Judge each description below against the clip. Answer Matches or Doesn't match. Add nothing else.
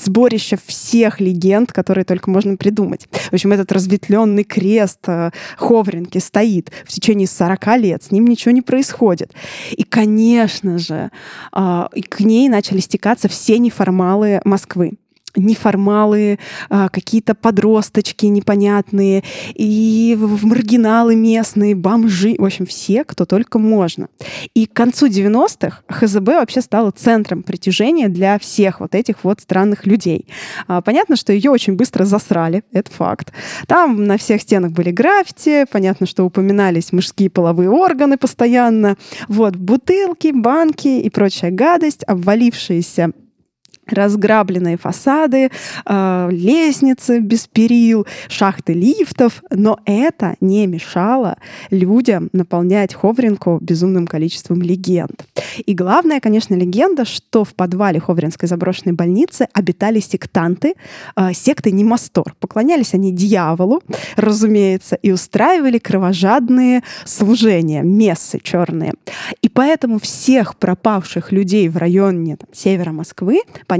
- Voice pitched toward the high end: Matches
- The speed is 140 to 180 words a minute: Doesn't match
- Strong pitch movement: Doesn't match